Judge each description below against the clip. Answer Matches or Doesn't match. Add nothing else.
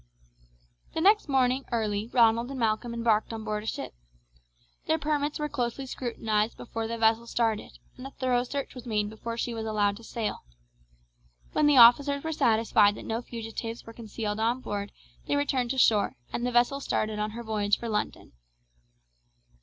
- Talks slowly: Doesn't match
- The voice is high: Matches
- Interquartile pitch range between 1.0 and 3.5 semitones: Matches